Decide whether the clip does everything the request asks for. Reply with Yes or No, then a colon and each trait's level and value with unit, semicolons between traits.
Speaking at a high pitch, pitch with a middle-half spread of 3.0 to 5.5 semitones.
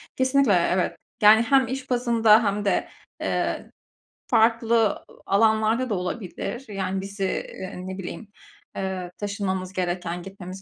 Yes: high, 200 Hz; average, 3.5 semitones